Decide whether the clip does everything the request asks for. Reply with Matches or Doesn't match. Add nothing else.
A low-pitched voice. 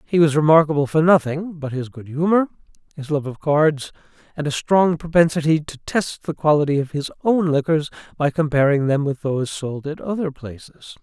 Doesn't match